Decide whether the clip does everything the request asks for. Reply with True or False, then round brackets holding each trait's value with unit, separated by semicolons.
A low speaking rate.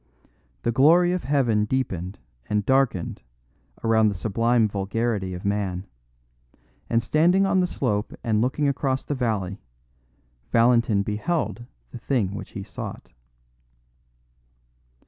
True (120 wpm)